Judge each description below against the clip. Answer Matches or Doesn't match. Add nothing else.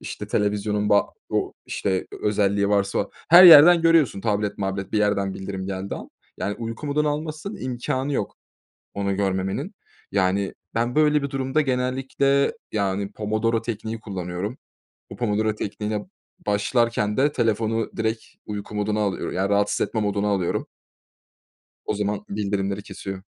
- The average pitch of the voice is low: Matches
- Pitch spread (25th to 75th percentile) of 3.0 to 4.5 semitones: Matches